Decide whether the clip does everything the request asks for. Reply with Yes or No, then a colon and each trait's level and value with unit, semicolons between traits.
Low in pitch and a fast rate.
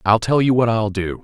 Yes: low, 110 Hz; fast, 290 wpm